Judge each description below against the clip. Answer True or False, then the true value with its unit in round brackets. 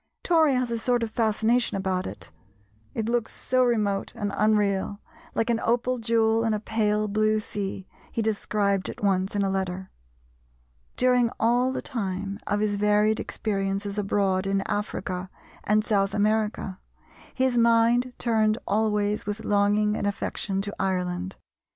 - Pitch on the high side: True (210 Hz)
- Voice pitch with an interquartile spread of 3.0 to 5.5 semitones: False (2.4 semitones)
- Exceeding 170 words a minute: False (150 wpm)